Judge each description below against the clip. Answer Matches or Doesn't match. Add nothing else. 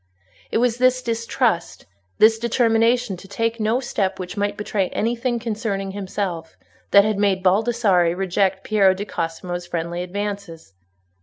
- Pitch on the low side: Doesn't match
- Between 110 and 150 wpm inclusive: Matches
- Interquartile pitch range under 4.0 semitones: Matches